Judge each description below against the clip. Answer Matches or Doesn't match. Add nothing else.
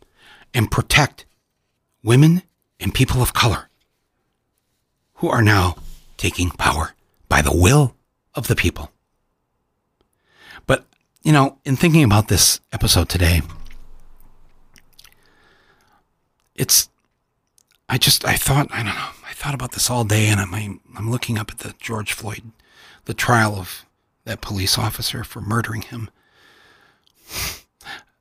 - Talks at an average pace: Doesn't match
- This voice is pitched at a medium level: Doesn't match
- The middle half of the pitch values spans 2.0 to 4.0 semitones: Doesn't match